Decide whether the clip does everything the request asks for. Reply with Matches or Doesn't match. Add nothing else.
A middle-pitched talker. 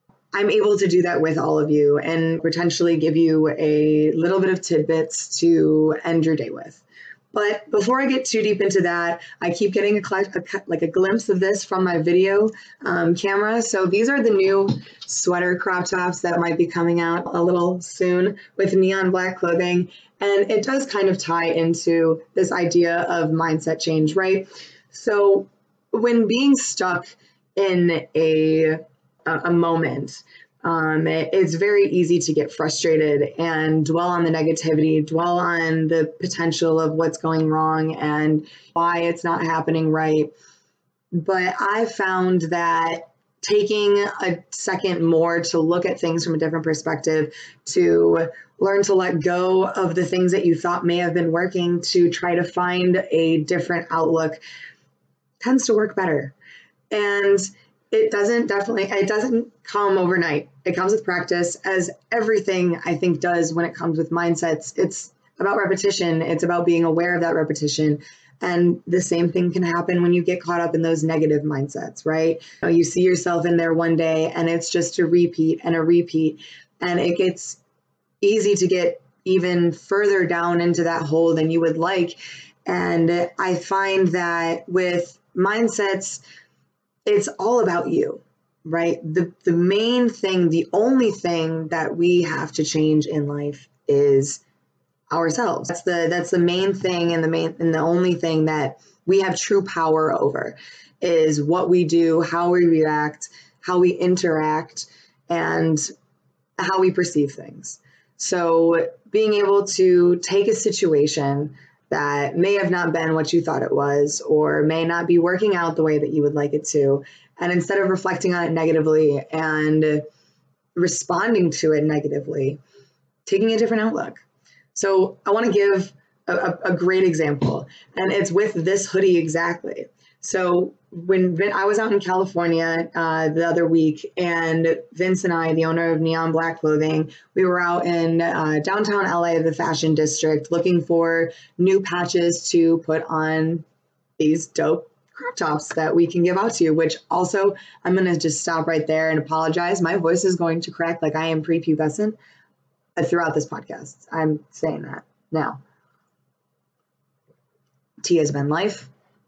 Matches